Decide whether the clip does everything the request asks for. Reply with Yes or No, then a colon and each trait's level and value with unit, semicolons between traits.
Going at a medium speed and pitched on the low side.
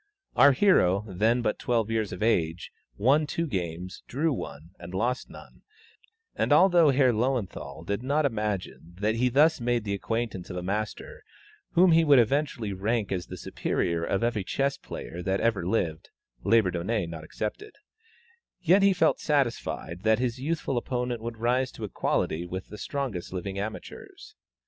Yes: average, 165 wpm; low, 110 Hz